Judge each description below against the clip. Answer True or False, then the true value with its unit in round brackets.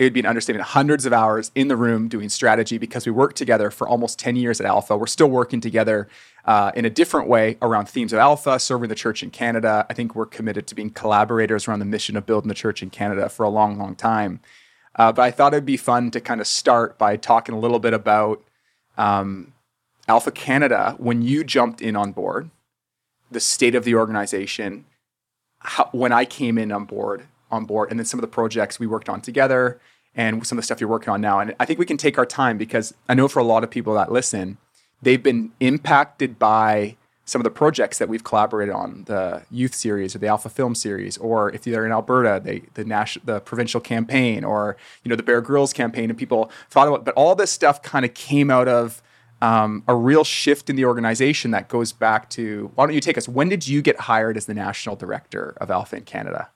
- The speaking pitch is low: True (115 Hz)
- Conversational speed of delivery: False (230 wpm)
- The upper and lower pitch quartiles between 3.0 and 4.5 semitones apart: False (2.6 semitones)